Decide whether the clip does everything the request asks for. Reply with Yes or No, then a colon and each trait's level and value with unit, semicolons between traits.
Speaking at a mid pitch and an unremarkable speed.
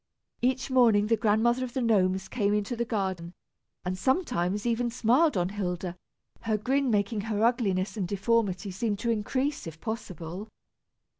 No: high, 215 Hz; average, 155 wpm